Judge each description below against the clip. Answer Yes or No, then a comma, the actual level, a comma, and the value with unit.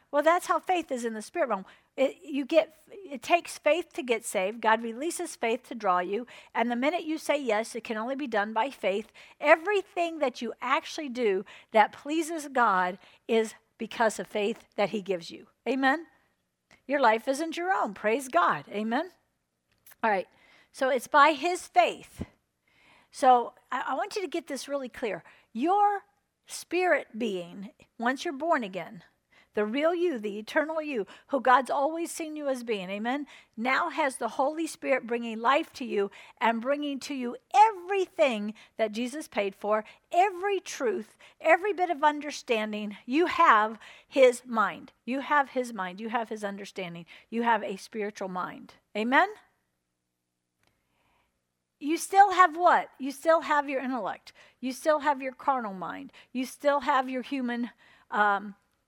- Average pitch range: No, wide, 6.4 semitones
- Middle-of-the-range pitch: No, very high, 260 Hz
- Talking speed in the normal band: Yes, average, 165 wpm